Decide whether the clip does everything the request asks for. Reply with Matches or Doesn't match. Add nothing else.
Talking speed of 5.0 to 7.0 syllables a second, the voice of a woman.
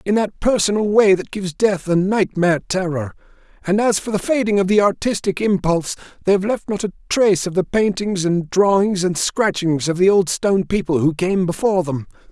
Doesn't match